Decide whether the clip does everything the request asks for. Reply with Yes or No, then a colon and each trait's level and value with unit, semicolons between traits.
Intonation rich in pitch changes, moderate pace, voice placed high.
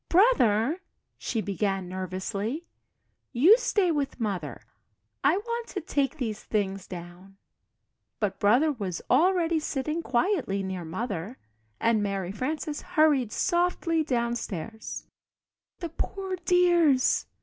No: wide, 8.3 semitones; slow, 100 wpm; high, 235 Hz